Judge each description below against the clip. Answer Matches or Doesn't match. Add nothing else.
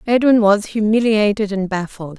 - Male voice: Doesn't match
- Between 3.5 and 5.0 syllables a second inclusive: Matches